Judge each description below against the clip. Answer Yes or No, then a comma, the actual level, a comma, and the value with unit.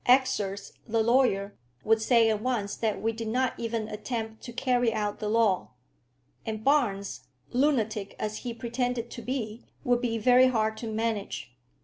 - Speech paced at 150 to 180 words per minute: Yes, average, 160 wpm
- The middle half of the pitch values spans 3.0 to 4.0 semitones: No, narrow, 2.4 semitones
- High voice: Yes, high, 225 Hz